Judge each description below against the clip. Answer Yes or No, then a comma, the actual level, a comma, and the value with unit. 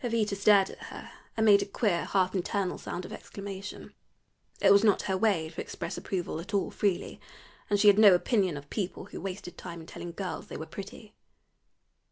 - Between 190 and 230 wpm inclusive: Yes, average, 200 wpm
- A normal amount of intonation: No, narrow, 2.3 semitones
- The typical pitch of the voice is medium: No, high, 195 Hz